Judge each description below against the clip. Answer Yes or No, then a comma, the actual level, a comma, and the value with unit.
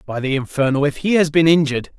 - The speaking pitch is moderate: Yes, medium, 150 Hz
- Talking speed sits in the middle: No, fast, 210 wpm